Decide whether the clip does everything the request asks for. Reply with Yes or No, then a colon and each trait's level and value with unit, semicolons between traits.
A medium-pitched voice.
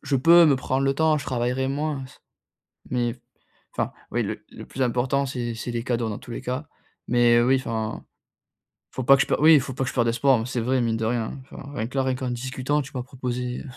No: low, 130 Hz